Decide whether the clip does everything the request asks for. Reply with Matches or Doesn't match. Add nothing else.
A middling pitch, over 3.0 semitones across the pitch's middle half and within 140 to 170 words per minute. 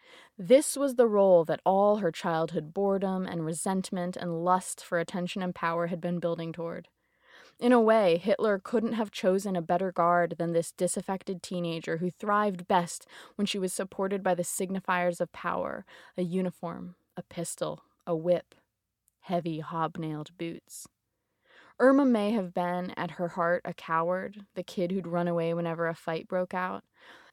Doesn't match